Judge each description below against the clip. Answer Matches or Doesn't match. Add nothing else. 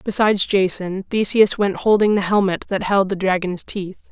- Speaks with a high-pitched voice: Matches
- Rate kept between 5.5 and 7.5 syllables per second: Doesn't match